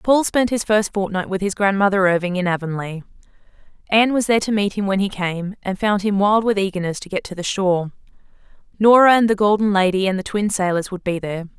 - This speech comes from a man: No, female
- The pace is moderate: No, fast, 220 wpm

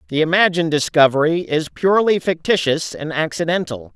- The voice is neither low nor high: Yes, medium, 160 Hz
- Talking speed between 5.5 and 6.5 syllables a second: Yes, 5.6 syllables/s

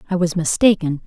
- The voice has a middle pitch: Yes, medium, 175 Hz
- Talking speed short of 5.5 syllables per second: No, 5.9 syllables/s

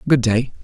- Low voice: Yes, low, 125 Hz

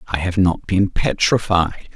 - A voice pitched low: Yes, very low, 90 Hz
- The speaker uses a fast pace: No, average, 155 wpm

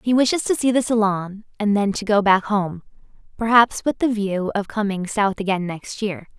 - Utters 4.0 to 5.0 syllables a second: Yes, 4.9 syllables/s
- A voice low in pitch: No, high, 210 Hz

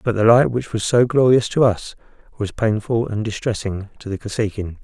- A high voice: No, low, 110 Hz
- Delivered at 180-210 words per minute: Yes, average, 200 wpm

